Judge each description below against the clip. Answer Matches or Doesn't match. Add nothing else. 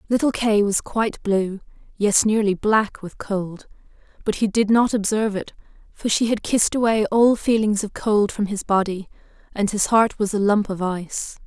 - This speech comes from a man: Doesn't match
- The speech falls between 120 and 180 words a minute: Doesn't match